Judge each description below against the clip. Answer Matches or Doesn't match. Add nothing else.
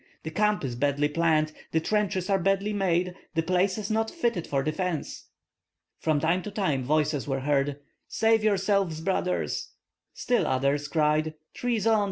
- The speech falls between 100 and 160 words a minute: Matches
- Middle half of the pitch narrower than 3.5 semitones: Doesn't match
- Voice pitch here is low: Doesn't match